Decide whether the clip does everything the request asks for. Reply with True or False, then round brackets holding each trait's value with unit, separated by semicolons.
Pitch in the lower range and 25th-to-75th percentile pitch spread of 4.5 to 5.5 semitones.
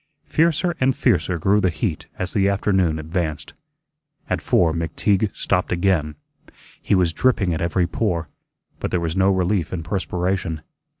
False (90 Hz; 3.1 semitones)